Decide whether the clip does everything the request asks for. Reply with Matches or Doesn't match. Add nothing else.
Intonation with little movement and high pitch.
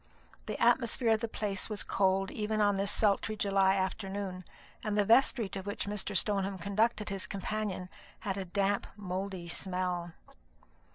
Matches